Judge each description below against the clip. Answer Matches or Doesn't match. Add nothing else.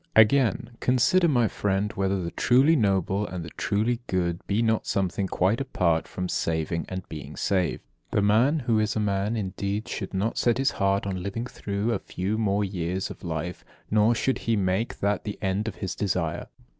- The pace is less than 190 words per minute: Doesn't match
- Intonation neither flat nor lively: Matches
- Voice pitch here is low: Matches